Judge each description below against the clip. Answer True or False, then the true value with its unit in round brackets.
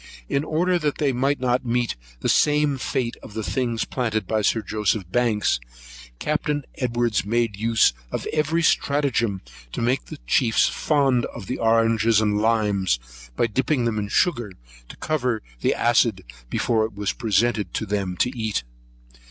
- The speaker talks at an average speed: True (160 wpm)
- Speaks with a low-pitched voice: True (115 Hz)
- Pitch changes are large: False (3.6 semitones)